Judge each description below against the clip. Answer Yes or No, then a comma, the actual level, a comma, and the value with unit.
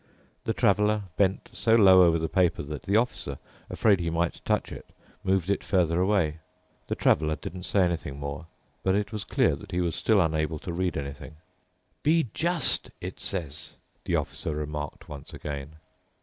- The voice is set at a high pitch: No, very low, 90 Hz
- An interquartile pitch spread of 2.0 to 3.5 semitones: No, average, 4.6 semitones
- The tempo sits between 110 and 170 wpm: No, average, 180 wpm